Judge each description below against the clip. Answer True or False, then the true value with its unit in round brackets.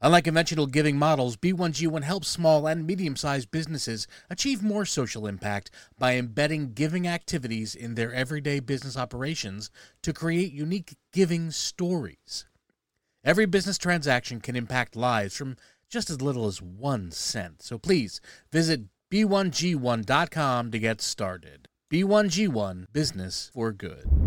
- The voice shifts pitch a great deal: True (6.7 semitones)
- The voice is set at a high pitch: False (145 Hz)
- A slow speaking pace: True (130 wpm)